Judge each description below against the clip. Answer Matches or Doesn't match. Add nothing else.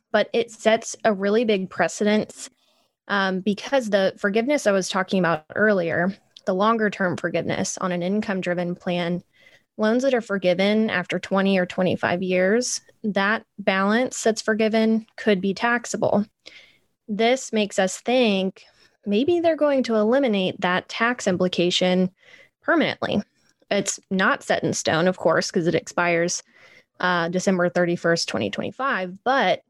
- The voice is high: Matches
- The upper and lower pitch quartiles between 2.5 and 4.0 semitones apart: Matches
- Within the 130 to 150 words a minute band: Matches